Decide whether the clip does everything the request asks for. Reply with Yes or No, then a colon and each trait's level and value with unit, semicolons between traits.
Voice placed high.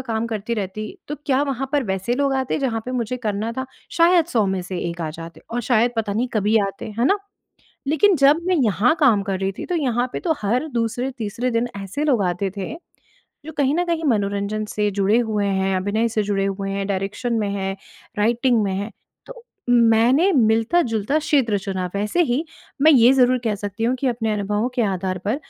Yes: high, 225 Hz